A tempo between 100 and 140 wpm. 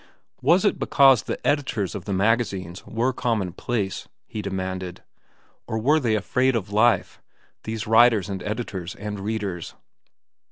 Yes: slow, 135 wpm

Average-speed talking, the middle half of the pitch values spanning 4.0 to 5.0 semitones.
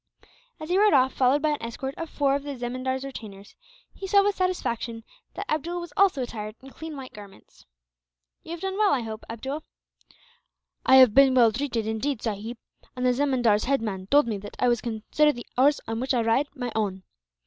No: fast, 210 wpm; average, 4.5 semitones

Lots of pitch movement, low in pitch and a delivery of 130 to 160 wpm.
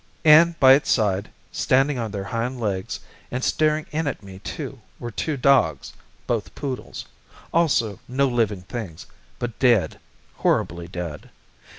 Yes: wide, 5.8 semitones; low, 120 Hz; average, 145 wpm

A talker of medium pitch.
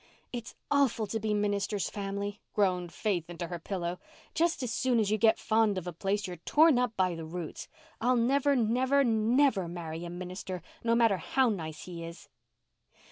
No: high, 205 Hz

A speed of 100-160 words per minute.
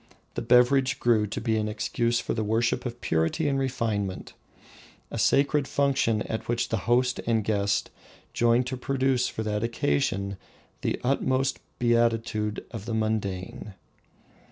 Yes: average, 145 wpm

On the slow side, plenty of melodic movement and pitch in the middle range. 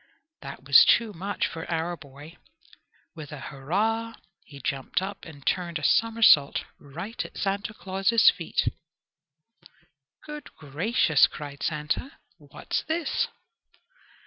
Yes: slow, 120 wpm; wide, 6.3 semitones; medium, 170 Hz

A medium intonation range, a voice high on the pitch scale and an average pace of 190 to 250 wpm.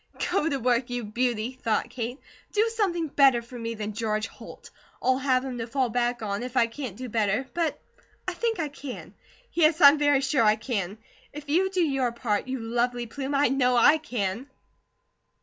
Yes: average, 3.7 semitones; very high, 250 Hz; average, 195 wpm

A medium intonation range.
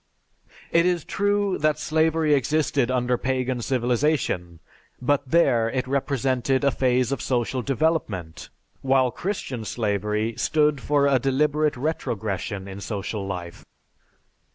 Yes: average, 4.5 semitones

